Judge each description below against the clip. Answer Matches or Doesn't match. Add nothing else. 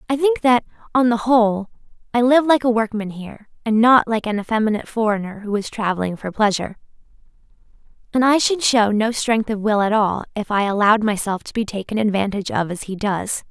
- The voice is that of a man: Doesn't match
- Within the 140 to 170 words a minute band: Doesn't match